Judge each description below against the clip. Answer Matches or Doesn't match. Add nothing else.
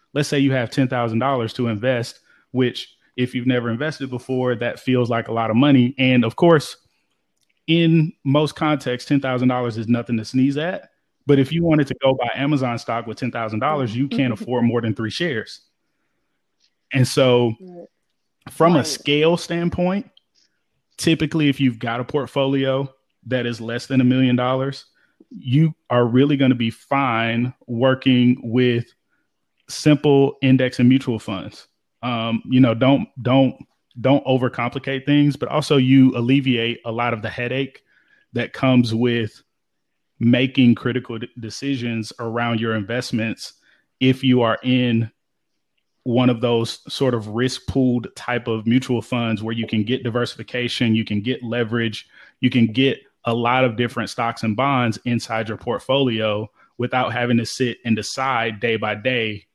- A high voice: Doesn't match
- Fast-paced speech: Doesn't match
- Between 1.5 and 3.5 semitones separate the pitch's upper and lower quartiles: Matches